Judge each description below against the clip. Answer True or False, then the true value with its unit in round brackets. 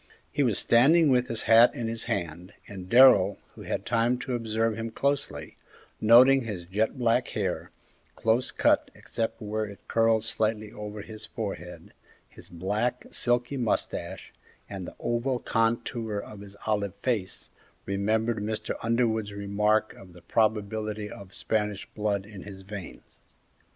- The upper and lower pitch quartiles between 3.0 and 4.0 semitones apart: False (2.4 semitones)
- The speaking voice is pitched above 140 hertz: False (110 Hz)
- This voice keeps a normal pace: True (145 wpm)